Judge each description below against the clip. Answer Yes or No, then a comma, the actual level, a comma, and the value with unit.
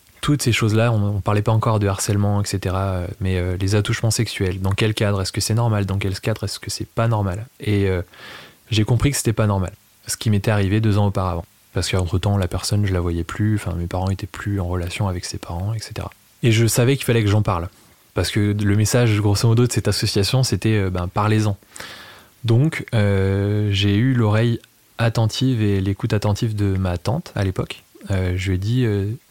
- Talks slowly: No, average, 215 wpm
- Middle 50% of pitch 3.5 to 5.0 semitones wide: No, average, 2.7 semitones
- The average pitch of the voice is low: Yes, low, 105 Hz